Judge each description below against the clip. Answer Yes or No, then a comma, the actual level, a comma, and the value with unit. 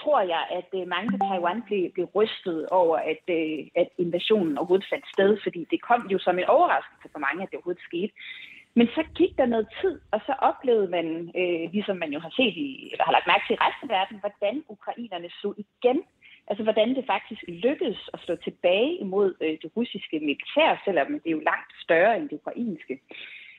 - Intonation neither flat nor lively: No, wide, 6.0 semitones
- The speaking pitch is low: No, high, 205 Hz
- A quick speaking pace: No, average, 200 wpm